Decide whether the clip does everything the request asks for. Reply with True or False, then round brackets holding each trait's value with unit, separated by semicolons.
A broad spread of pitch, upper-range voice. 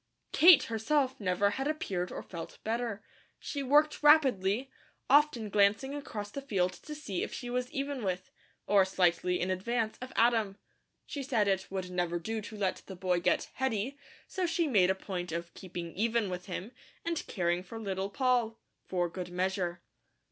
True (5.9 semitones; 205 Hz)